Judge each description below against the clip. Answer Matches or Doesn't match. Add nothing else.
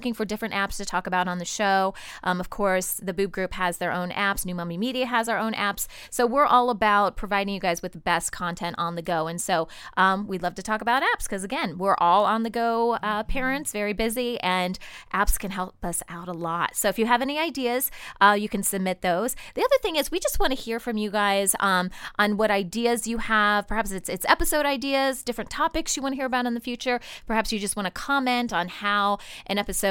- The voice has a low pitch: Doesn't match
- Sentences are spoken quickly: Matches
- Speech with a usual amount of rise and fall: Matches